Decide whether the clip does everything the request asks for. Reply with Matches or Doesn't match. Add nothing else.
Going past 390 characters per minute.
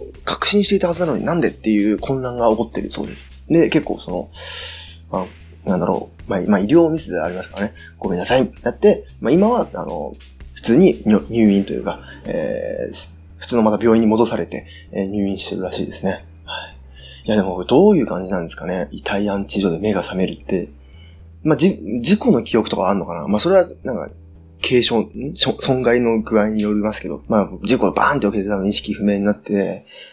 Matches